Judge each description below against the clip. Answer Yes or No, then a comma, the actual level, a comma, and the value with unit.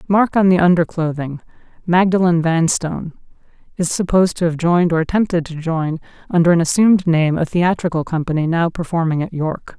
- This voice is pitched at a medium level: Yes, medium, 170 Hz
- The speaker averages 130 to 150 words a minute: No, average, 160 wpm